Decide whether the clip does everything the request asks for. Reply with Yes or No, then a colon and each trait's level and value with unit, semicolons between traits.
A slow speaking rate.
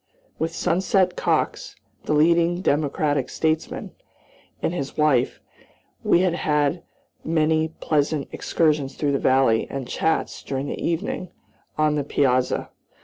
Yes: slow, 120 wpm